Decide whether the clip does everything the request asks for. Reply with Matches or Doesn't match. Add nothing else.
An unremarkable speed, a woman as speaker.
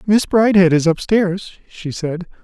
Doesn't match